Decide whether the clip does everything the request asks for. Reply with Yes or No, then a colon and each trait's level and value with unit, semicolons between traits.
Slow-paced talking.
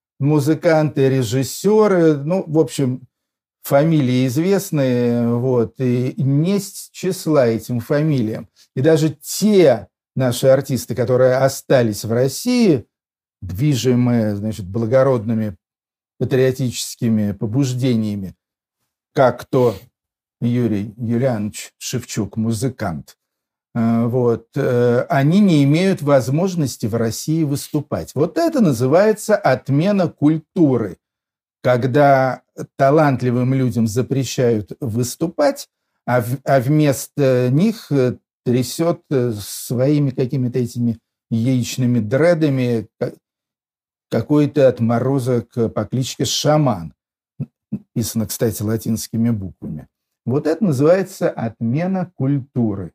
Yes: slow, 85 wpm